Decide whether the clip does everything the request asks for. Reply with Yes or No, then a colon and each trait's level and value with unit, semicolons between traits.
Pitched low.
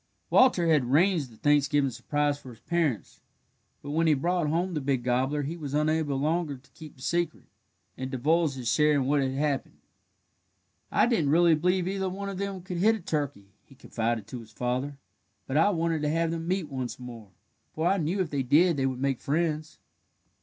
No: medium, 150 Hz